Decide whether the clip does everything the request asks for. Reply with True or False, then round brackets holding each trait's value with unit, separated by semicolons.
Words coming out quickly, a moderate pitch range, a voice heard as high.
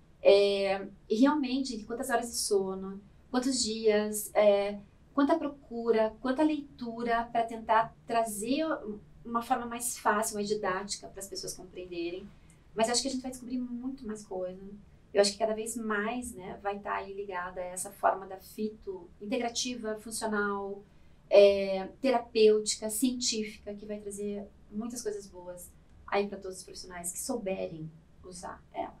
False (155 wpm; 3.0 semitones; 215 Hz)